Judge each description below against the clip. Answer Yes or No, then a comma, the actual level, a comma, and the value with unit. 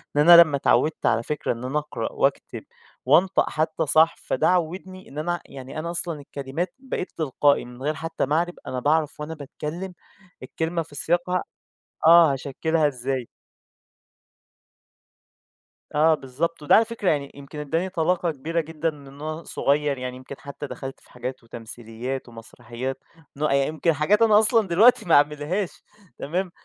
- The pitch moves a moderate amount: Yes, average, 3.6 semitones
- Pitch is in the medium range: Yes, medium, 150 Hz